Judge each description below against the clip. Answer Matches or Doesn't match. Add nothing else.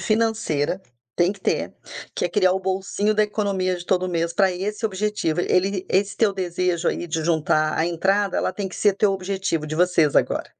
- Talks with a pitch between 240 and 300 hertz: Doesn't match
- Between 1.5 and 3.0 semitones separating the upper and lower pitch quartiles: Matches